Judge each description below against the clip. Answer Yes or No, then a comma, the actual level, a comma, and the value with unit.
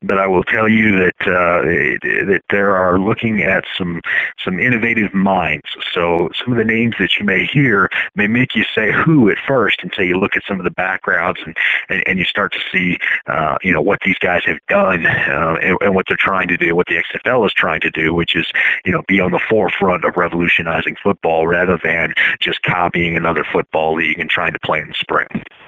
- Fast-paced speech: Yes, fast, 220 wpm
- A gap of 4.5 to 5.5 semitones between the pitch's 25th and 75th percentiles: No, average, 3.5 semitones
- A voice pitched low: Yes, very low, 90 Hz